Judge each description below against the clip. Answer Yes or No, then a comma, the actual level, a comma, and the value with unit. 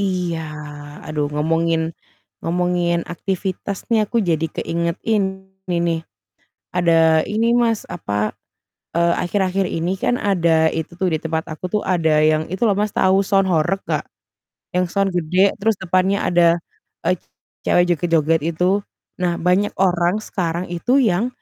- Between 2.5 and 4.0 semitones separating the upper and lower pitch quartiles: Yes, average, 2.8 semitones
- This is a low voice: No, medium, 180 Hz